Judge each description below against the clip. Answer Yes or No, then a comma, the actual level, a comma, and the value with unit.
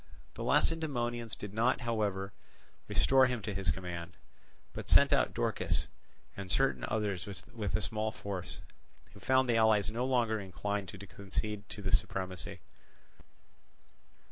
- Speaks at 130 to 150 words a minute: Yes, average, 145 wpm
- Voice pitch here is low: Yes, low, 105 Hz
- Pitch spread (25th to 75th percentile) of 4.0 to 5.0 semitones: No, average, 3.4 semitones